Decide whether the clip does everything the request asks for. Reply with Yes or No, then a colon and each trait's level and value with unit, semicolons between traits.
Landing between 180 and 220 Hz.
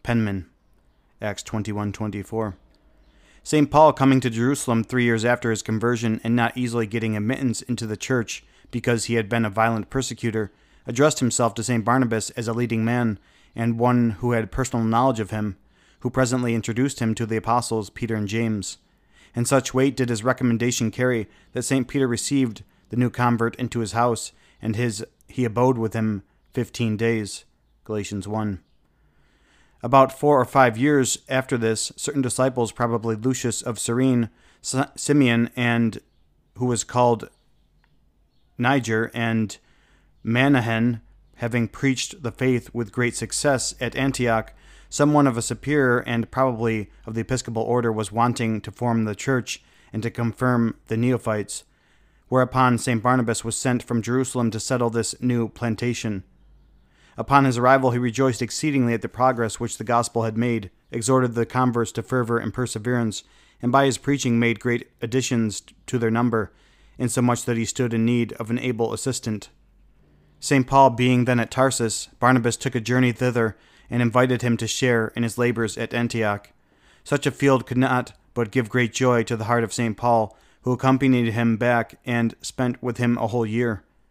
No: low, 120 Hz